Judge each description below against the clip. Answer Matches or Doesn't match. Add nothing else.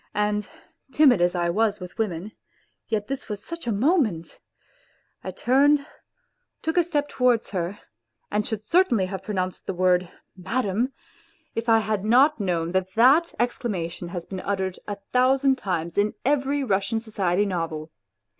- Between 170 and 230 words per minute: Doesn't match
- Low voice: Doesn't match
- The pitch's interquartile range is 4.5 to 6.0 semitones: Matches